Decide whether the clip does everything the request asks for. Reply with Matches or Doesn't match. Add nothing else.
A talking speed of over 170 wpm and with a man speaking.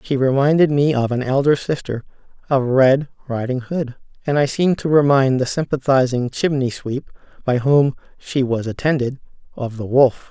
Doesn't match